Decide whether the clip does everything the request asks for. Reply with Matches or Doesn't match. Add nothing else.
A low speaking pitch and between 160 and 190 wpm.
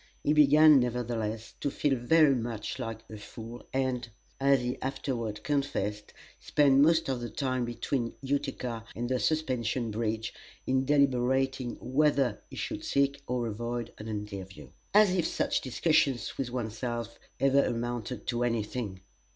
Doesn't match